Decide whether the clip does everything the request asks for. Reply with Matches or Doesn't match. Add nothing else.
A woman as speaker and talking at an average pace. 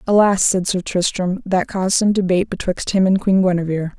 Matches